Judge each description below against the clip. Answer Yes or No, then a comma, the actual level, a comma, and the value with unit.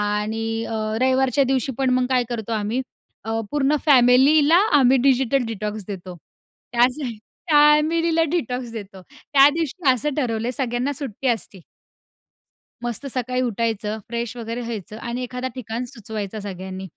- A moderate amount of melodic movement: Yes, average, 3.4 semitones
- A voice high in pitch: Yes, high, 245 Hz